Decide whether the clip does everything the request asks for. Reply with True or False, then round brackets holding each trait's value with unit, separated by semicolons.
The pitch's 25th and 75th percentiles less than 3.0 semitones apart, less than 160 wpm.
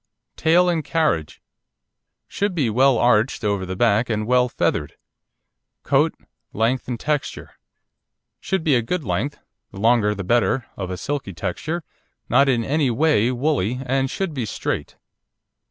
False (5.6 semitones; 150 wpm)